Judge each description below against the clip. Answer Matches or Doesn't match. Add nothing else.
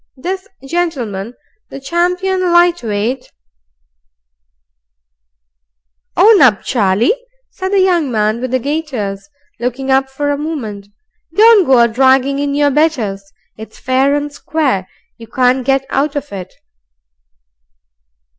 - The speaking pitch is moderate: Doesn't match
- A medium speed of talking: Doesn't match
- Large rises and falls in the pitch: Matches